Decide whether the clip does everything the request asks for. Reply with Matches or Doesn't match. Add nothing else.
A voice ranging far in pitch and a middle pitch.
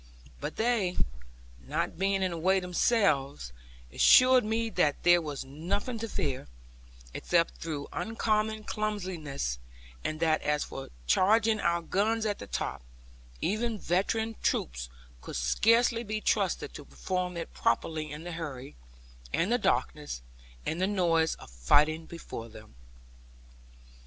Matches